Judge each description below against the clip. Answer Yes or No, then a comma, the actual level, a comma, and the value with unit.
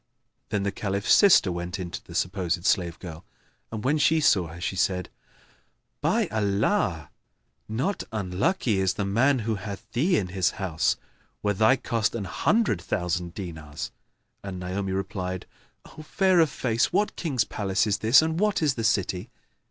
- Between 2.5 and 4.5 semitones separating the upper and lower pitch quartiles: No, average, 5.2 semitones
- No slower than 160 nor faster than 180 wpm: Yes, average, 165 wpm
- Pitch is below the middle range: Yes, low, 100 Hz